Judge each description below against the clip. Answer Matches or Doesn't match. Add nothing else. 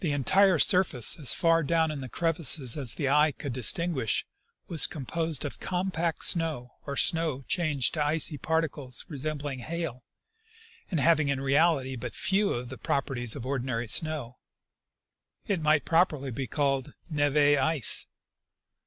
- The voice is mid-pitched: Matches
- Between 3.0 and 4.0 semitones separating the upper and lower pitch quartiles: Matches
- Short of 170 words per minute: Matches